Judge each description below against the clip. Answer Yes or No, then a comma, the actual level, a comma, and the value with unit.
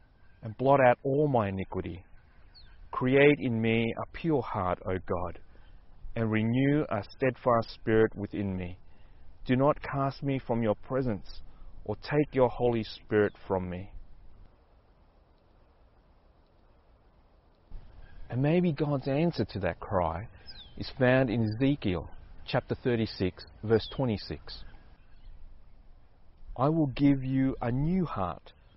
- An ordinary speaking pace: No, slow, 120 wpm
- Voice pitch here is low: Yes, low, 105 Hz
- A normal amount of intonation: No, wide, 6.5 semitones